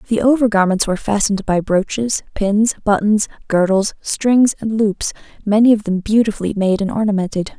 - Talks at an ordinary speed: Yes, average, 160 wpm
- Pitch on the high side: Yes, high, 210 Hz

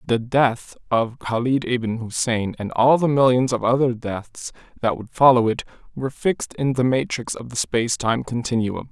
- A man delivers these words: Yes, male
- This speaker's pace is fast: No, average, 180 wpm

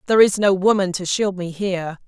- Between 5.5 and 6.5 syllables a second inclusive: Yes, 6.0 syllables/s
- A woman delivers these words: Yes, female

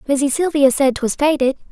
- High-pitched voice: Yes, very high, 280 Hz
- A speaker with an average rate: Yes, average, 175 wpm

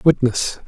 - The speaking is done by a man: Yes, male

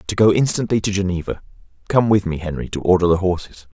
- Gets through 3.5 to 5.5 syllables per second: No, 6.4 syllables/s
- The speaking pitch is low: Yes, very low, 95 Hz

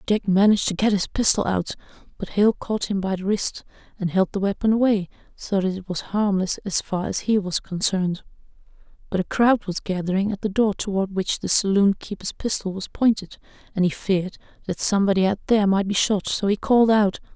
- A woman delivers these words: Yes, female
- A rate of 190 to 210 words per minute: Yes, fast, 205 wpm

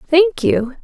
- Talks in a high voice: Yes, very high, 325 Hz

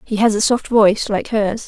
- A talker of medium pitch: No, high, 215 Hz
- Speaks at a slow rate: No, fast, 250 wpm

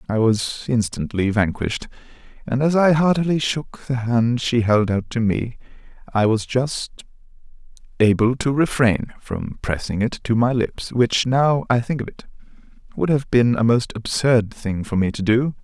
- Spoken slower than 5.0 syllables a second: Yes, 4.5 syllables/s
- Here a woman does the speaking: No, male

